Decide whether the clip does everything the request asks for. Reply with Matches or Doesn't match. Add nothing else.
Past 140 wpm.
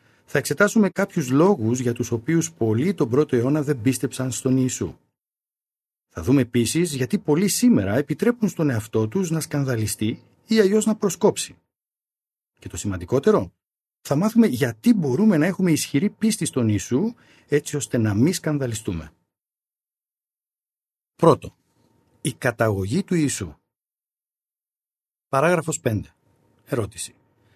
Doesn't match